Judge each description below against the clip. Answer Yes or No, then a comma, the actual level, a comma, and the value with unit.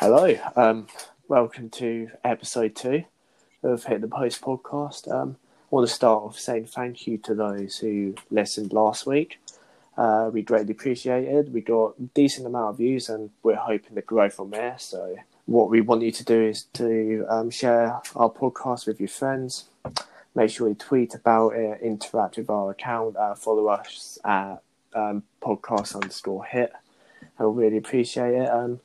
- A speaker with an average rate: Yes, average, 175 wpm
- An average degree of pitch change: No, narrow, 2.2 semitones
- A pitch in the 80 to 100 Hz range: No, low, 115 Hz